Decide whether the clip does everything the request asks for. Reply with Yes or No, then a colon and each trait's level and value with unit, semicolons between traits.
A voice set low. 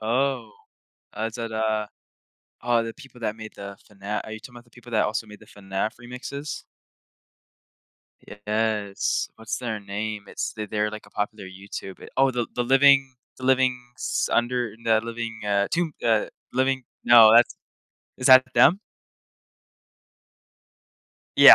Yes: low, 115 Hz